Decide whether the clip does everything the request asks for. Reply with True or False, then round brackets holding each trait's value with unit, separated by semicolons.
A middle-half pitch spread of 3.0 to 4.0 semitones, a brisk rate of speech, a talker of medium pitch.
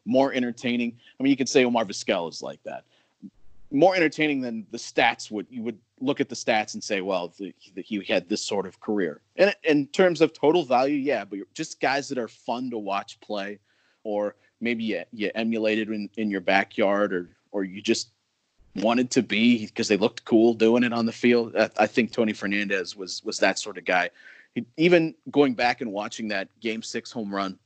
False (3.6 semitones; 215 wpm; 115 Hz)